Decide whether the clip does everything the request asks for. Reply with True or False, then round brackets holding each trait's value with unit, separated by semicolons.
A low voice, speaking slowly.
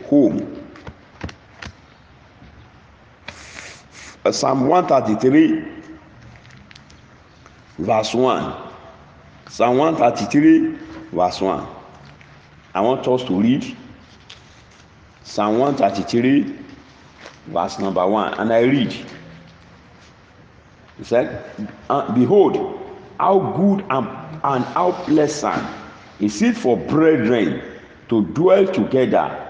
False (155 Hz; 90 wpm)